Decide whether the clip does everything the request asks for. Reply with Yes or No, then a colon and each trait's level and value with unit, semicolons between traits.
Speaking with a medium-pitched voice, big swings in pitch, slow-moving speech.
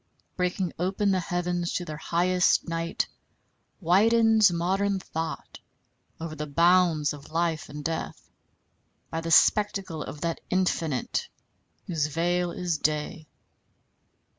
No: medium, 170 Hz; narrow, 2.4 semitones; slow, 115 wpm